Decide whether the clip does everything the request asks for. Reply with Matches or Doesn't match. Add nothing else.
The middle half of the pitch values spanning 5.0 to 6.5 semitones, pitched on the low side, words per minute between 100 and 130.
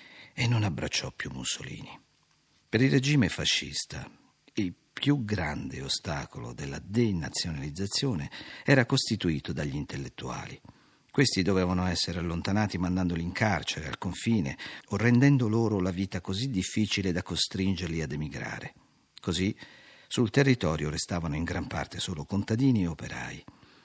Matches